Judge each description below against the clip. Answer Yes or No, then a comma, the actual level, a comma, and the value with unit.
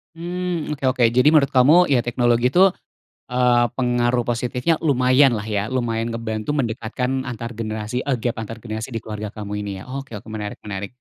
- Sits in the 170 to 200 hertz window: No, low, 120 Hz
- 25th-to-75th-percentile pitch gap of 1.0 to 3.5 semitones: Yes, average, 2.9 semitones